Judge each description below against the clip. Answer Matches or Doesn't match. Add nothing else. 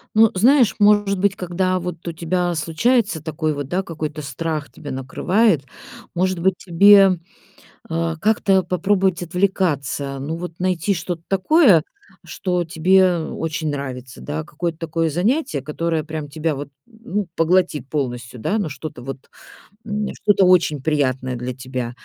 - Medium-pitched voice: Matches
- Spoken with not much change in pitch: Doesn't match